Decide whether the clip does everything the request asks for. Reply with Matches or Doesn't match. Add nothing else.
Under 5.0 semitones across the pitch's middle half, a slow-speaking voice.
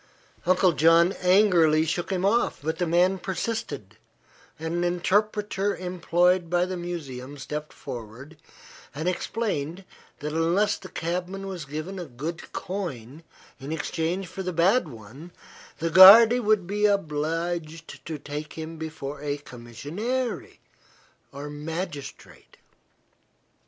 Matches